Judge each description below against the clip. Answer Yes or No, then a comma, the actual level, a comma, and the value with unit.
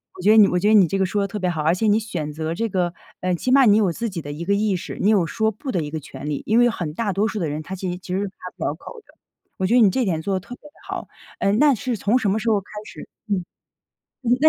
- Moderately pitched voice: No, high, 195 Hz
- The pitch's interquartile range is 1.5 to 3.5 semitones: No, average, 3.9 semitones